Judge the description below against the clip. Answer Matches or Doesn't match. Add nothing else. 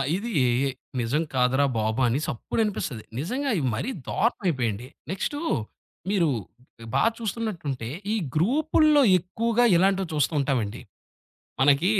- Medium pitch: Matches